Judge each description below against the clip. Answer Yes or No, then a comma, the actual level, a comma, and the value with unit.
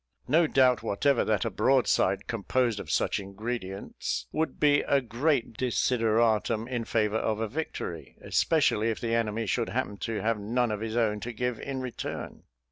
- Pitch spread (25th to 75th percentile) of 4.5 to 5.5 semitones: No, average, 2.9 semitones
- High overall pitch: No, low, 115 Hz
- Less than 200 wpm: Yes, average, 170 wpm